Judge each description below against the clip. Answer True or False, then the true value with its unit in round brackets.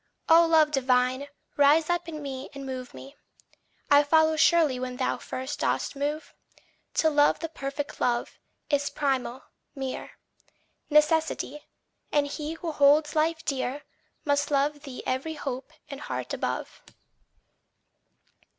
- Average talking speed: False (130 wpm)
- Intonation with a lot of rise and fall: False (2.5 semitones)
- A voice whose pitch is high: True (290 Hz)